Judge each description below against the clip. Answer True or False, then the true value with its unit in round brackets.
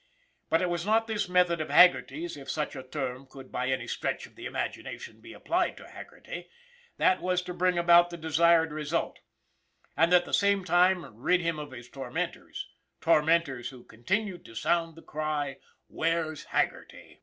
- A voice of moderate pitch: True (165 Hz)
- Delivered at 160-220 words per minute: True (180 wpm)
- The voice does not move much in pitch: False (3.8 semitones)